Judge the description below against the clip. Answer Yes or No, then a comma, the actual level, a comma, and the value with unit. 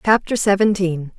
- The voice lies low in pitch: No, high, 195 Hz